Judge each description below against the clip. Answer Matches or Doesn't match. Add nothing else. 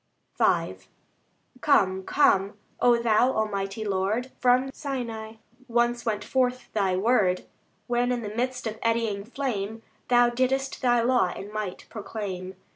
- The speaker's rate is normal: Doesn't match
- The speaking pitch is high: Matches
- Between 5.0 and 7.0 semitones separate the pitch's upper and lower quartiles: Doesn't match